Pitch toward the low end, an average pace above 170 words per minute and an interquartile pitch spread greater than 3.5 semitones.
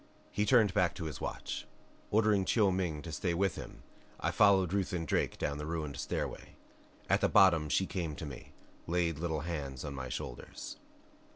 Yes: very low, 85 Hz; average, 185 wpm; average, 4.1 semitones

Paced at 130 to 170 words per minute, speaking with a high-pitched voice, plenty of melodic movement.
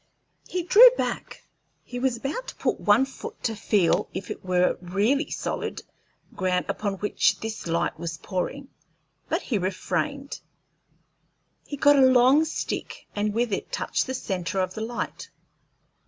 Yes: average, 155 wpm; high, 220 Hz; wide, 6.3 semitones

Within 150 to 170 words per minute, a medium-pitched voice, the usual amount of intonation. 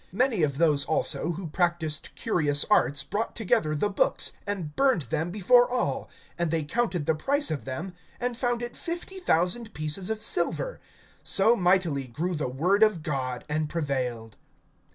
No: average, 165 wpm; medium, 170 Hz; wide, 6.6 semitones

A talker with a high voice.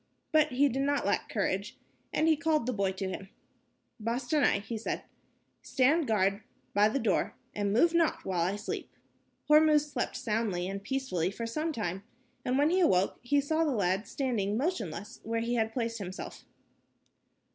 Yes: high, 230 Hz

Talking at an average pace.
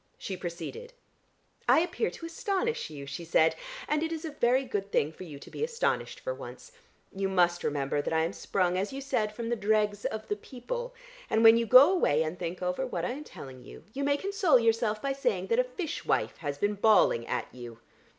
No: fast, 220 wpm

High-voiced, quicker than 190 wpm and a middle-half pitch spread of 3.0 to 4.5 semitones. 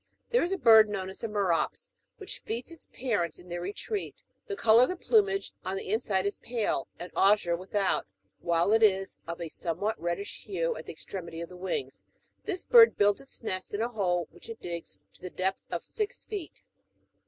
No: high, 205 Hz; fast, 205 wpm; wide, 5.4 semitones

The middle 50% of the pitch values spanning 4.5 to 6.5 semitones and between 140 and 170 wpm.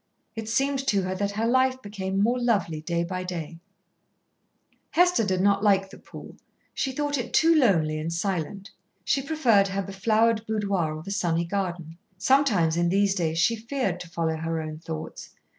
No: average, 5.1 semitones; average, 190 wpm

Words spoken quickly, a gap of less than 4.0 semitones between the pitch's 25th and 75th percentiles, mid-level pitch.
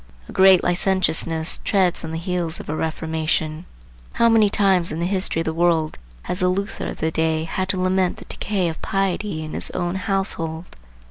No: average, 195 wpm; average, 2.9 semitones; medium, 175 Hz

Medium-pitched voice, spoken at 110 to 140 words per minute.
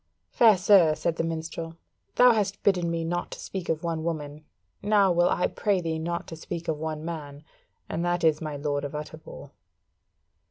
No: medium, 165 Hz; average, 185 wpm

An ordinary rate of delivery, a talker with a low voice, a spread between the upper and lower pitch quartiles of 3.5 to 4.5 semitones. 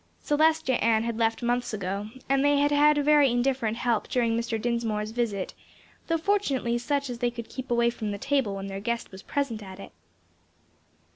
No: average, 190 wpm; high, 240 Hz; average, 4.0 semitones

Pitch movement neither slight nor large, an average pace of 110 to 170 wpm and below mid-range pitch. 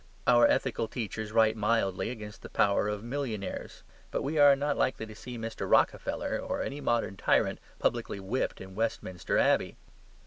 Yes: average, 3.1 semitones; average, 165 wpm; low, 115 Hz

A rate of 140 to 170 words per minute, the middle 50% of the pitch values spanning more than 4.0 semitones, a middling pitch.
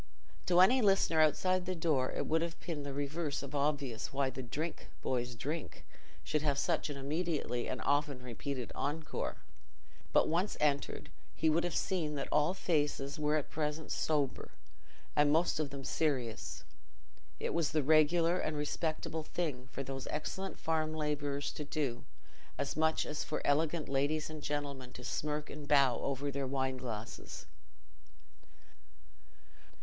No: average, 155 wpm; narrow, 2.4 semitones; medium, 150 Hz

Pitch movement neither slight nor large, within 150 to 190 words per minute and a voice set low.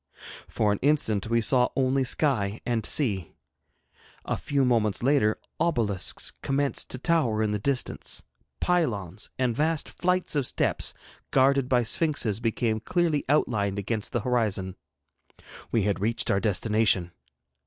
No: average, 4.8 semitones; slow, 135 wpm; low, 115 Hz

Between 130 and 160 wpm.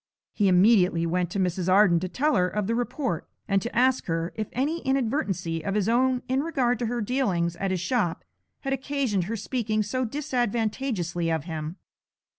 No: average, 185 wpm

